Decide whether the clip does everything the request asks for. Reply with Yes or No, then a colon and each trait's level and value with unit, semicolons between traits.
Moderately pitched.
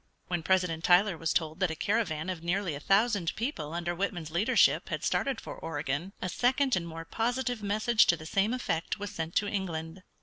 Yes: medium, 180 Hz